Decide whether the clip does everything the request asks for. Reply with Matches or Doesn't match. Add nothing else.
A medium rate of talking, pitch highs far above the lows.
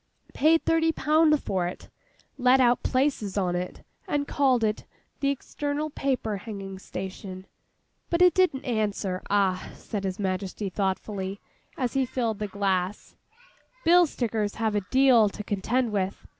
Matches